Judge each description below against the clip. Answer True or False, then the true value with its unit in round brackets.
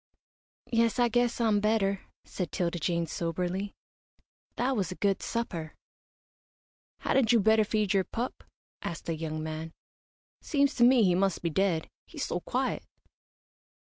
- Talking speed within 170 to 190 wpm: False (145 wpm)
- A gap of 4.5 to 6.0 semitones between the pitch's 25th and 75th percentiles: True (5.3 semitones)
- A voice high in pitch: True (195 Hz)